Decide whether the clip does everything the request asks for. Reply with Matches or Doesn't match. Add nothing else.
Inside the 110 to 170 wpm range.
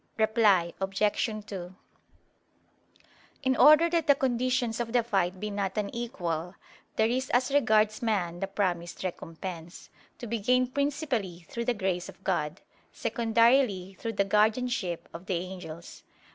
Matches